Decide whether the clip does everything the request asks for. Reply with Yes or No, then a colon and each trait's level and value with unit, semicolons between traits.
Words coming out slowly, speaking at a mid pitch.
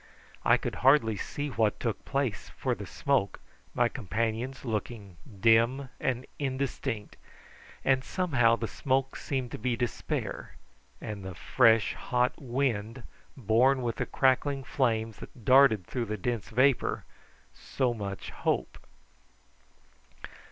No: slow, 125 wpm; low, 120 Hz